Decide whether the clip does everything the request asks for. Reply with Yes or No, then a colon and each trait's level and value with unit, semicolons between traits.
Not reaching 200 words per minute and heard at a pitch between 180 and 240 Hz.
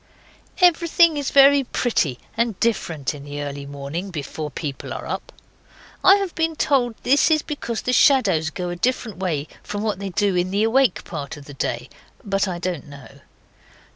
Yes: average, 180 wpm; high, 190 Hz